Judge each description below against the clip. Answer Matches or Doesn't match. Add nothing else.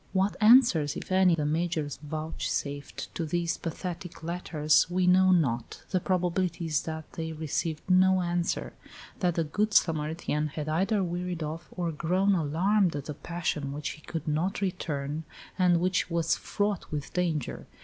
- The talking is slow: Doesn't match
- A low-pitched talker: Doesn't match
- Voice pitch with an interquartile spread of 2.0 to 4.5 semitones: Matches